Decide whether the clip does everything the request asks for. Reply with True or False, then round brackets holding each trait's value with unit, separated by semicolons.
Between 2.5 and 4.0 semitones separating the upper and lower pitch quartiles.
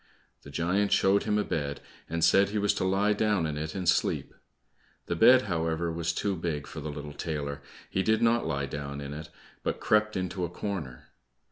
False (5.2 semitones)